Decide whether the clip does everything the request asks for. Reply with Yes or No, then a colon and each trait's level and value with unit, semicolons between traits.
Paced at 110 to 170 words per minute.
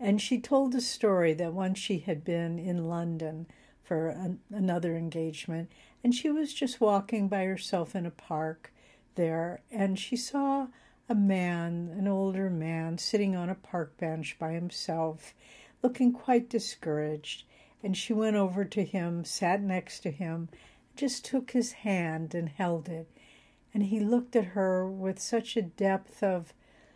Yes: average, 160 wpm